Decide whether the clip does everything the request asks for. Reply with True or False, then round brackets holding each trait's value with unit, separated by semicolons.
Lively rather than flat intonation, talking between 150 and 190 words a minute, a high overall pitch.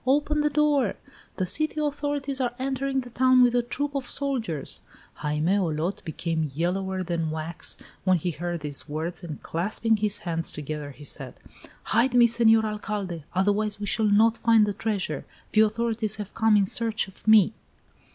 True (5.9 semitones; 170 wpm; 210 Hz)